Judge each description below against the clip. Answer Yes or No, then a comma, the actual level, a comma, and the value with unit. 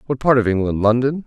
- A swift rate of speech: No, average, 190 wpm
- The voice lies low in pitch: Yes, low, 120 Hz